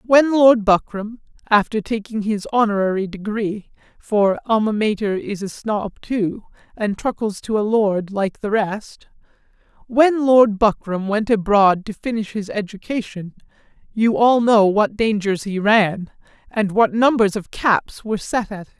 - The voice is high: Yes, high, 210 Hz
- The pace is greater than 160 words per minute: No, average, 150 wpm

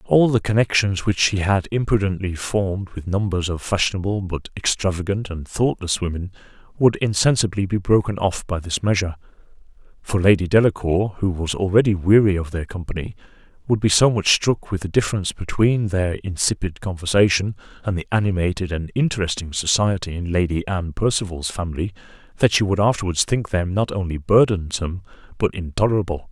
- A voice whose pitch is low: Yes, very low, 95 Hz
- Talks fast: No, average, 155 wpm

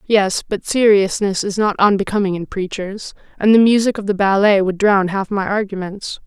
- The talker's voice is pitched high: Yes, high, 200 Hz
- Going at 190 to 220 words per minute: No, average, 180 wpm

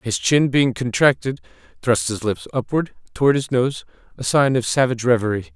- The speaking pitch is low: Yes, low, 120 Hz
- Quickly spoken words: No, average, 175 wpm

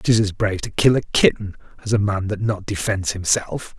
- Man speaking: Yes, male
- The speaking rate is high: Yes, fast, 220 wpm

